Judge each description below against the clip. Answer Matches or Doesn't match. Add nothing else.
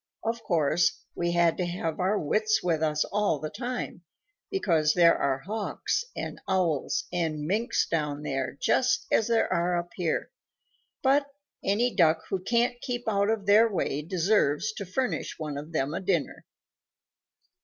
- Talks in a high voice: Doesn't match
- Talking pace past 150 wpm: Matches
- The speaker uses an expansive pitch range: Matches